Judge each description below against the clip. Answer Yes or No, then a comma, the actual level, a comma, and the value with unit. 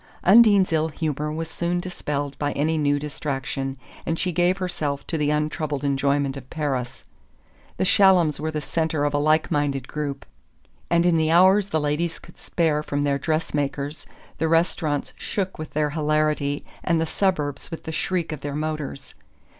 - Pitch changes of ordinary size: No, narrow, 2.3 semitones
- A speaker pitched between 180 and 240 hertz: No, medium, 155 Hz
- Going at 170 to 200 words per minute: Yes, average, 175 wpm